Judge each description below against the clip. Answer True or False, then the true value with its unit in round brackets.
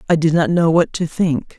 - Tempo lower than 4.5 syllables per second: False (5.0 syllables/s)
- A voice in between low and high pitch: True (165 Hz)